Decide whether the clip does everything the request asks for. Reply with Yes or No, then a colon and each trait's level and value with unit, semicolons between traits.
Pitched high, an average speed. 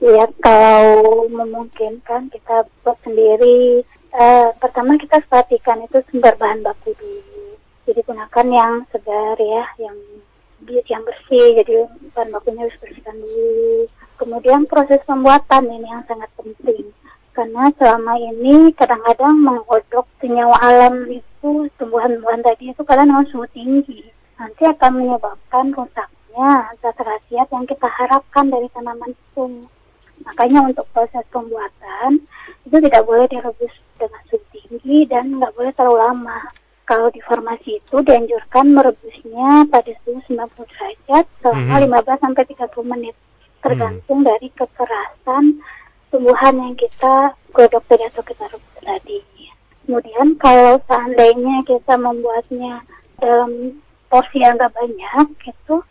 Yes: high, 245 Hz; average, 125 wpm